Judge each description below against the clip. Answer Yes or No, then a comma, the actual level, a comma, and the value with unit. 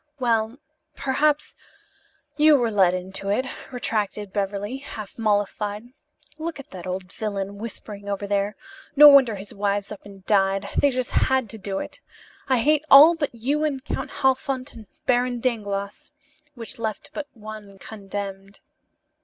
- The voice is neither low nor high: No, high, 215 Hz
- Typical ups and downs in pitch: Yes, average, 4.6 semitones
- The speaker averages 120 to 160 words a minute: Yes, average, 150 wpm